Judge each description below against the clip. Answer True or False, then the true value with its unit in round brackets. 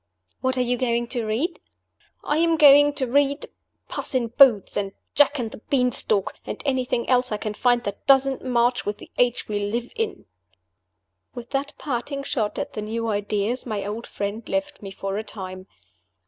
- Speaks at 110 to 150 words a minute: False (190 wpm)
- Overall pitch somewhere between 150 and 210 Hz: False (240 Hz)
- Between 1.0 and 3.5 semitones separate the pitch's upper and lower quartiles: False (4.3 semitones)